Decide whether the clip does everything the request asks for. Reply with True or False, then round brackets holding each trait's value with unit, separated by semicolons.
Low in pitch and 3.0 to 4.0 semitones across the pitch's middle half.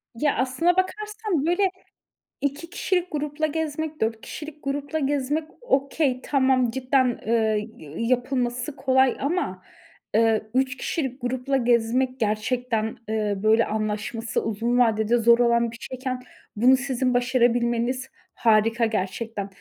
False (250 Hz; 3.5 semitones)